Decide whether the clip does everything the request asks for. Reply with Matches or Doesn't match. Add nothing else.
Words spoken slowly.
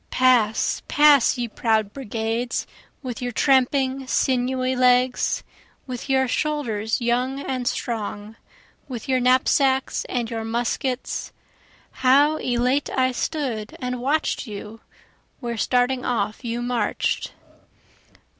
Matches